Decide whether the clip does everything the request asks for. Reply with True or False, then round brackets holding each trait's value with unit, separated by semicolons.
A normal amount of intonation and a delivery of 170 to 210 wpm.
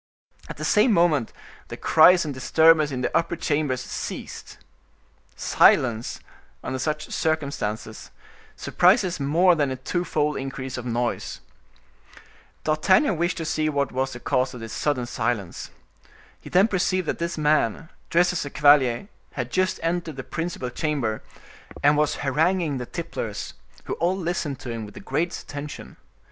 False (4.7 semitones; 155 wpm)